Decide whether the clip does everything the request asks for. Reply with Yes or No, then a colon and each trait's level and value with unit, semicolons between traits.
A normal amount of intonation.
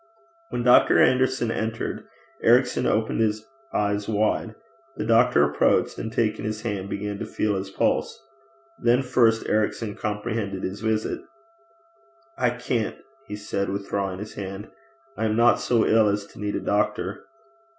No: narrow, 2.2 semitones